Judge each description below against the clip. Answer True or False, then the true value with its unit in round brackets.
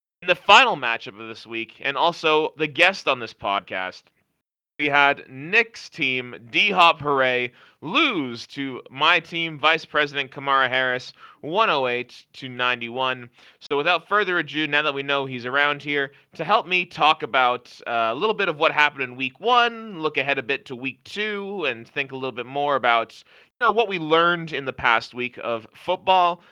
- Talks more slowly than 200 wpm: True (180 wpm)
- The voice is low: False (145 Hz)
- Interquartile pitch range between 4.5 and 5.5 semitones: True (5.1 semitones)